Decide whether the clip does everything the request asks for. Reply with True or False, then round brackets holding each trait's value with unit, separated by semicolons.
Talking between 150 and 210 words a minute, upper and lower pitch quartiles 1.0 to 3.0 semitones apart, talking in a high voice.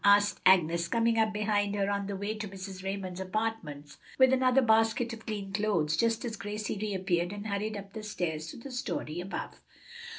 True (190 wpm; 2.7 semitones; 205 Hz)